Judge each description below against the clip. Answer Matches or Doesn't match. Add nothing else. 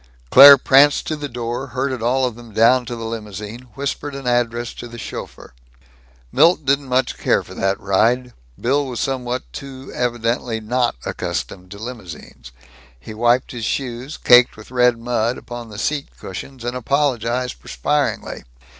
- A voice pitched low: Matches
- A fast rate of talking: Doesn't match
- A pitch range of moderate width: Doesn't match